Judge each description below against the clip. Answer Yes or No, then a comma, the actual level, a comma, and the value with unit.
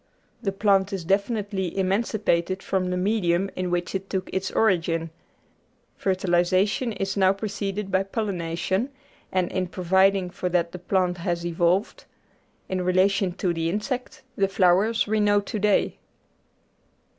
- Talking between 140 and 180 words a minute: Yes, average, 145 wpm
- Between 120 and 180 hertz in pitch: No, high, 190 Hz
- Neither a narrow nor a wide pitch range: No, narrow, 2.0 semitones